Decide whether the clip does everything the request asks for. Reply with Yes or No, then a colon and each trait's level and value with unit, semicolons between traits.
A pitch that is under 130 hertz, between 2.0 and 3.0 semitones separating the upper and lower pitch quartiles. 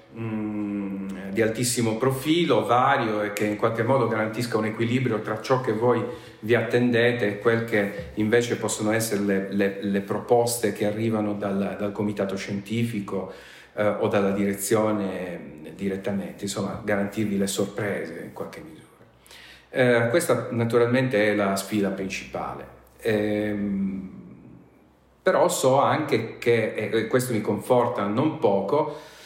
Yes: low, 105 Hz; narrow, 2.6 semitones